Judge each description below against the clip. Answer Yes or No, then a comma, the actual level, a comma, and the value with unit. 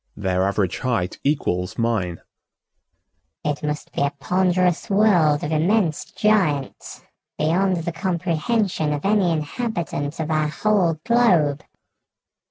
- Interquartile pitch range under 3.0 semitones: No, average, 4.8 semitones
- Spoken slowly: Yes, slow, 115 wpm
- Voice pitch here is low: No, medium, 160 Hz